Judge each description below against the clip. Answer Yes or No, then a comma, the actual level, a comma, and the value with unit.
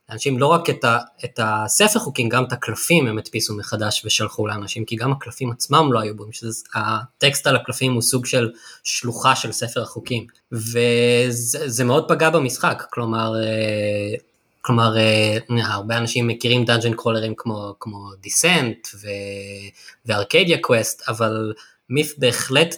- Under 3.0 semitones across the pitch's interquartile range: Yes, narrow, 2.6 semitones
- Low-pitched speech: Yes, low, 115 Hz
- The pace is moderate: Yes, average, 140 wpm